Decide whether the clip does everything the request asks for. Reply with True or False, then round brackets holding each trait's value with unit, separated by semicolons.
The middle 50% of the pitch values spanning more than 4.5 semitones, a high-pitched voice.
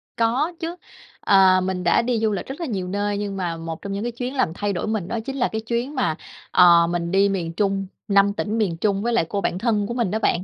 False (4.0 semitones; 200 Hz)